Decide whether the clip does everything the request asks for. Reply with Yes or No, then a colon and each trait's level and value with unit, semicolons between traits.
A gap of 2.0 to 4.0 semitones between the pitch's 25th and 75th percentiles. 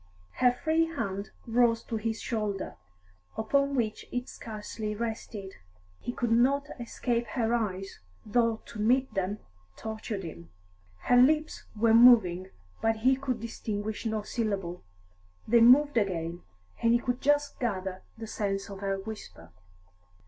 Yes: average, 3.3 semitones